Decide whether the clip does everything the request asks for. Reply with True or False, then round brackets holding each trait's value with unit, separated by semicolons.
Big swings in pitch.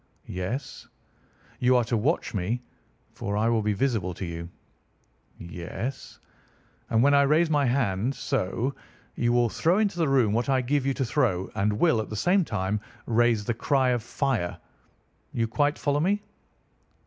False (4.8 semitones)